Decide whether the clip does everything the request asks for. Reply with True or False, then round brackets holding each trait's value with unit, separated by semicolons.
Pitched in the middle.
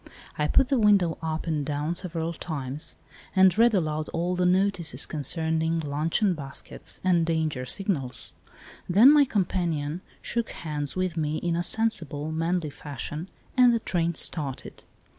True (165 Hz)